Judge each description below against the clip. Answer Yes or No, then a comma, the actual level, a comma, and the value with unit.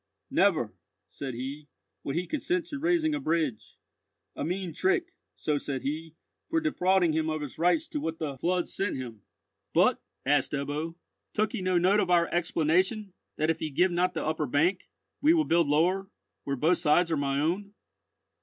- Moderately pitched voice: Yes, medium, 170 Hz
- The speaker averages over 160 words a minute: Yes, average, 180 wpm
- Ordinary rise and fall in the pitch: Yes, average, 4.5 semitones